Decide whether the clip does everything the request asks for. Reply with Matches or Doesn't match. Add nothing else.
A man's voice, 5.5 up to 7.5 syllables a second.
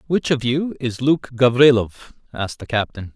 Doesn't match